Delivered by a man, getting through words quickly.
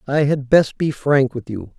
Yes: male; fast, 235 wpm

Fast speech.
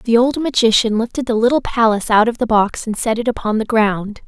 Yes: fast, 240 wpm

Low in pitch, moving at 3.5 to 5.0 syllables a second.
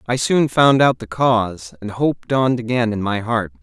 Yes: low, 115 Hz; 4.8 syllables/s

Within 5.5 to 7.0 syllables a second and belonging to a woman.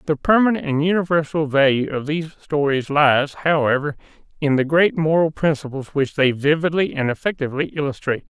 No: 5.6 syllables/s; male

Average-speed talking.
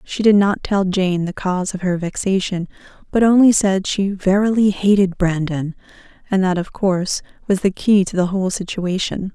Yes: average, 180 wpm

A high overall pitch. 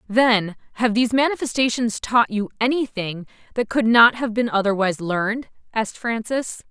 Yes: high, 225 Hz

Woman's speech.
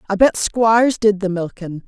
Yes: female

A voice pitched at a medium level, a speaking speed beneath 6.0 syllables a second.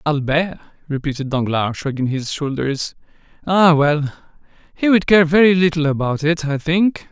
Yes: medium, 155 Hz; 4.8 syllables/s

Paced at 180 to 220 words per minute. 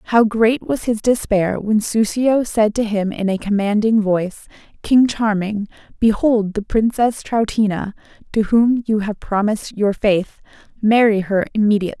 No: average, 150 wpm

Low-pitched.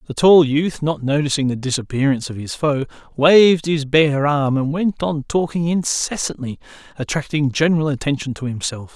No: medium, 145 Hz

